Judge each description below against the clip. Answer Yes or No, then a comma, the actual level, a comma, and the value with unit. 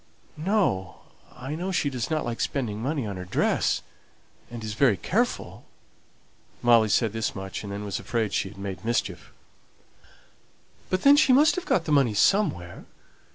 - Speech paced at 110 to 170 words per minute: Yes, average, 160 wpm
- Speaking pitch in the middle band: No, low, 115 Hz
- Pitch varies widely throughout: Yes, wide, 7.2 semitones